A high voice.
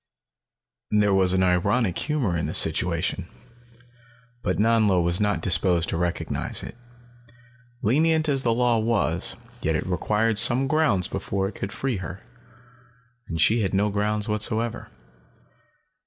No: low, 105 Hz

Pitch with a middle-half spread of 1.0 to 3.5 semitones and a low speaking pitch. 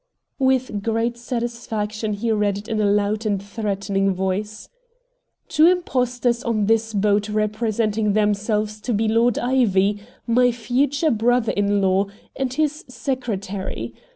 No: average, 3.0 semitones; high, 215 Hz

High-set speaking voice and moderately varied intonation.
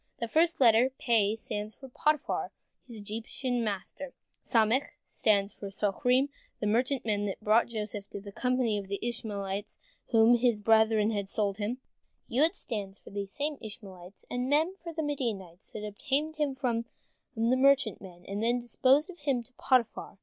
Yes: high, 225 Hz; average, 4.0 semitones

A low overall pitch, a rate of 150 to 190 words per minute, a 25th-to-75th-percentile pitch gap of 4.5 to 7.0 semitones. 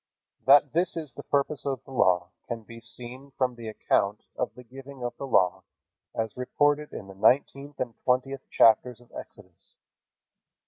No: low, 125 Hz; average, 170 wpm; average, 3.5 semitones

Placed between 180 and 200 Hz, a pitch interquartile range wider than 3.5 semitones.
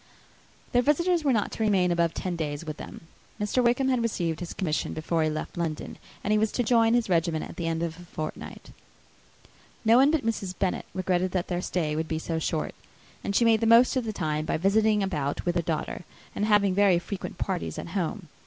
Yes: medium, 185 Hz; average, 5.1 semitones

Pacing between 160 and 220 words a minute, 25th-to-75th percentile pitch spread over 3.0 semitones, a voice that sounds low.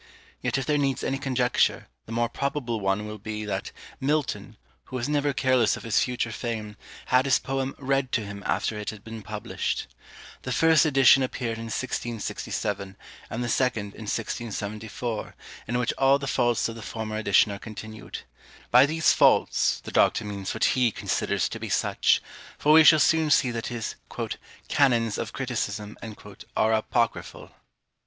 Yes: average, 170 wpm; average, 3.7 semitones; low, 120 Hz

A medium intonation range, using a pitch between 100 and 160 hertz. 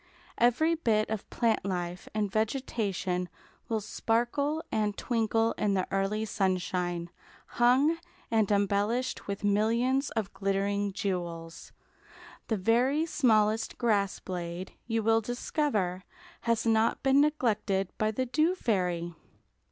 No: average, 3.7 semitones; high, 215 Hz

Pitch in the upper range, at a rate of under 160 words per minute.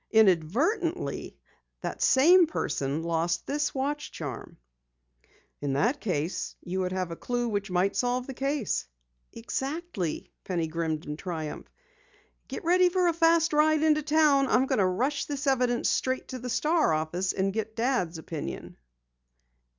Yes: high, 240 Hz; average, 150 wpm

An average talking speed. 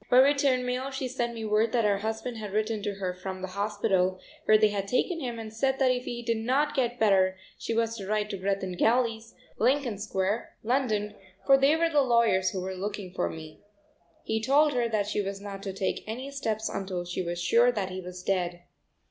No: fast, 225 wpm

